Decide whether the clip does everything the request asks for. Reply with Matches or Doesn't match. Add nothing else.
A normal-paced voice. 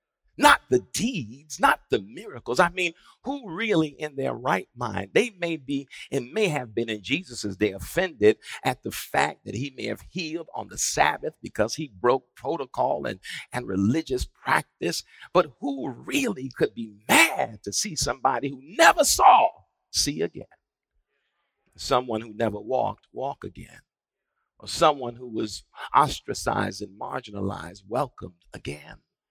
Matches